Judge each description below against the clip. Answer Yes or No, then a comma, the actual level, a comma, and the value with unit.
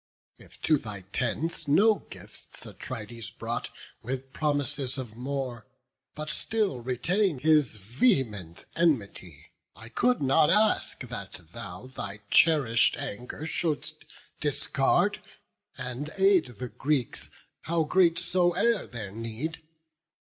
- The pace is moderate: No, slow, 115 wpm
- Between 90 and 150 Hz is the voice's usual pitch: Yes, low, 135 Hz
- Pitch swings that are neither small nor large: No, wide, 6.0 semitones